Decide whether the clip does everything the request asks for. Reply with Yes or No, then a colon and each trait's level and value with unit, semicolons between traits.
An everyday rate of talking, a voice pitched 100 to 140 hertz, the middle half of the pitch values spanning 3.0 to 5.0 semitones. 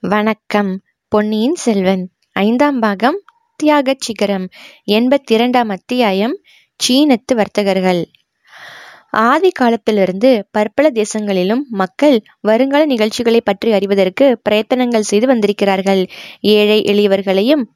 No: average, 90 wpm; high, 220 Hz; average, 4.3 semitones